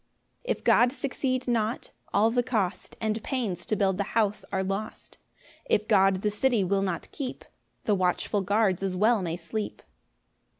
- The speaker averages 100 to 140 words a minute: No, average, 170 wpm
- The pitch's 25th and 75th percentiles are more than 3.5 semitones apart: No, average, 3.2 semitones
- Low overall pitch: No, high, 210 Hz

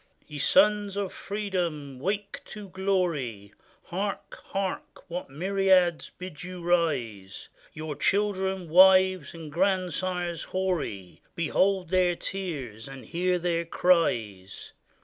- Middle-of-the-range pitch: Yes, medium, 180 Hz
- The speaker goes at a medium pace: No, slow, 110 wpm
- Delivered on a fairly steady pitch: No, average, 4.1 semitones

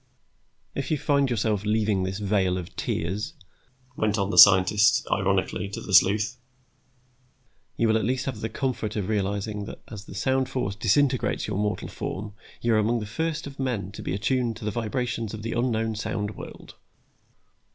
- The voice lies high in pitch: No, low, 110 Hz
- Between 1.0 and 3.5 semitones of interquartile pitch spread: Yes, average, 3.0 semitones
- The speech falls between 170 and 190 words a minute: Yes, average, 180 wpm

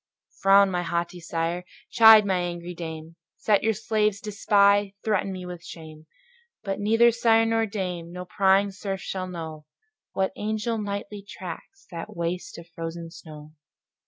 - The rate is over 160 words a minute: No, average, 155 wpm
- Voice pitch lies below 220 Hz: Yes, high, 190 Hz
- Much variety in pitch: No, average, 3.5 semitones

